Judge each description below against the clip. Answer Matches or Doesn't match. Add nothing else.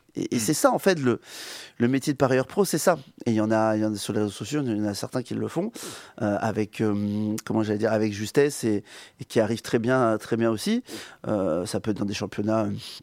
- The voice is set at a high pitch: Doesn't match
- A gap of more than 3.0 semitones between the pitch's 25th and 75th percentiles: Matches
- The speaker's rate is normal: Doesn't match